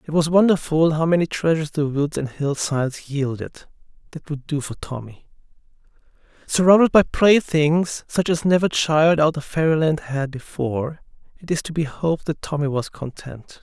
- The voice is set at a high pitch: No, medium, 155 Hz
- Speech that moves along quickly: No, average, 165 wpm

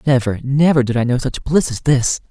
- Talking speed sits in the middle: No, fast, 235 wpm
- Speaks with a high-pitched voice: No, low, 130 Hz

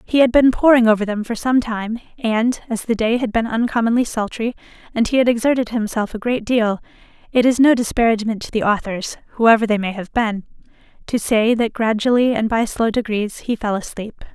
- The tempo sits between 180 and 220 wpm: Yes, average, 200 wpm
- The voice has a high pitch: Yes, high, 225 Hz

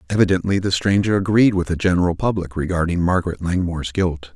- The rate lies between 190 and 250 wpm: No, average, 165 wpm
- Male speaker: Yes, male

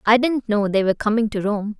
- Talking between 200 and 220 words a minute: No, fast, 265 wpm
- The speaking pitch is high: Yes, high, 215 Hz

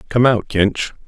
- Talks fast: No, average, 165 wpm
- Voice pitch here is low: Yes, low, 110 Hz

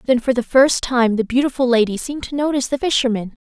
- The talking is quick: Yes, fast, 225 wpm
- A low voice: No, very high, 250 Hz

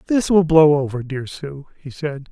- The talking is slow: No, fast, 205 wpm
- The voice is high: No, medium, 150 Hz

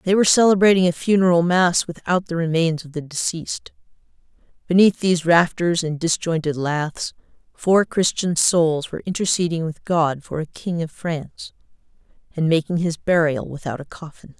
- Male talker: No, female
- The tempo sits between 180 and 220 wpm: No, average, 155 wpm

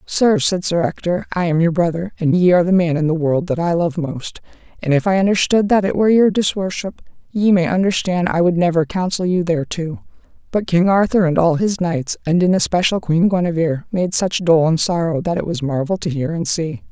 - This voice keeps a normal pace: No, fast, 225 wpm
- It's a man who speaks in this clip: No, female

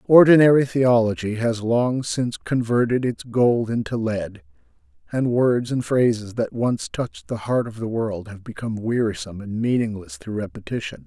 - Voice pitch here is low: Yes, low, 115 Hz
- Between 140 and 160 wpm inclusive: Yes, average, 155 wpm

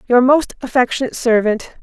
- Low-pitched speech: No, high, 245 Hz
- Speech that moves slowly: Yes, slow, 130 wpm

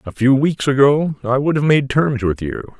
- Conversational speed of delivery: No, fast, 235 wpm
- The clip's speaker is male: Yes, male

